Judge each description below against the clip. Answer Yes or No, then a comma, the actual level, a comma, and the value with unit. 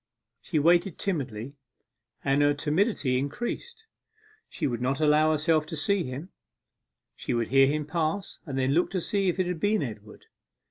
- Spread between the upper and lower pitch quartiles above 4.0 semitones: Yes, average, 4.8 semitones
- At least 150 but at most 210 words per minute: Yes, average, 170 wpm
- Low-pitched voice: No, medium, 155 Hz